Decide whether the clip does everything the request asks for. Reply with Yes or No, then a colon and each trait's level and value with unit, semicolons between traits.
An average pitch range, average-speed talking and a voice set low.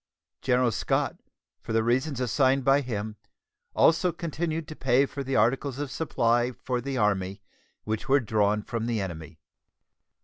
Yes: average, 4.0 semitones; average, 150 wpm; low, 125 Hz